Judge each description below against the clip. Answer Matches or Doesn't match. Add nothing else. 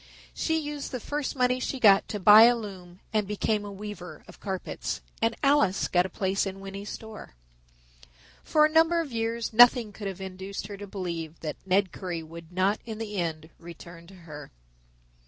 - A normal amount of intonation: Matches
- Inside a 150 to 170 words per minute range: Doesn't match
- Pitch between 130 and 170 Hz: Doesn't match